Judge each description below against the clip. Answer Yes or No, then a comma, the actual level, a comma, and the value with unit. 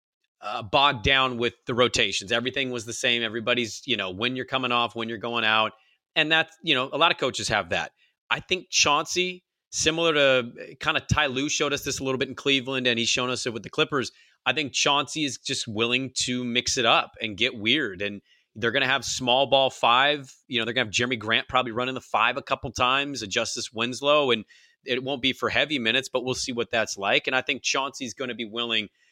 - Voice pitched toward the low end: Yes, low, 125 Hz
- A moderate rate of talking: No, fast, 235 wpm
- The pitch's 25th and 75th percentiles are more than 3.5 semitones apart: No, average, 2.9 semitones